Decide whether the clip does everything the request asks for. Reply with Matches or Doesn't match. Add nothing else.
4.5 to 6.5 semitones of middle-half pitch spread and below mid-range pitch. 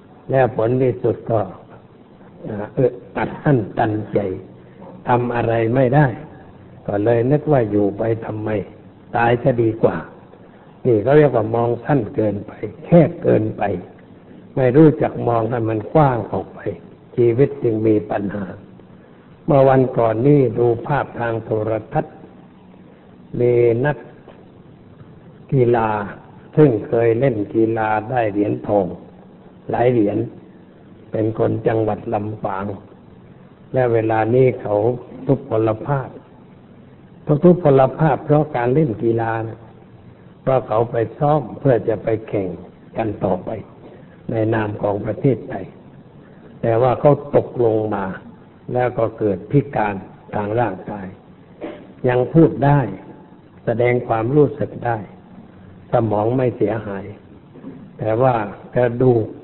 Doesn't match